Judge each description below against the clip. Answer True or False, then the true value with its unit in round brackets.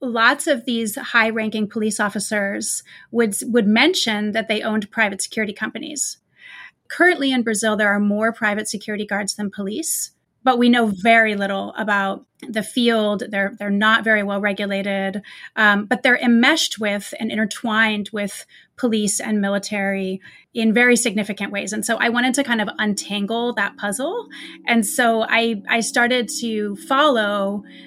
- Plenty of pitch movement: False (2.7 semitones)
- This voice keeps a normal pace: True (155 wpm)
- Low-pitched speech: False (220 Hz)